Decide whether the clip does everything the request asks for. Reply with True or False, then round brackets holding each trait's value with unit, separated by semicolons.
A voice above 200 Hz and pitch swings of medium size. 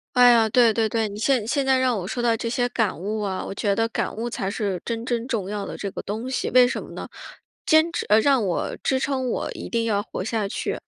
True (230 Hz; 3.2 semitones)